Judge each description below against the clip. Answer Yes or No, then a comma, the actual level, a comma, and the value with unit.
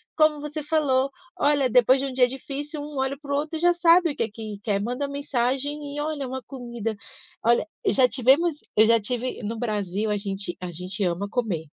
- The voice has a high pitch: Yes, very high, 260 Hz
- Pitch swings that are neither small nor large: Yes, average, 4.9 semitones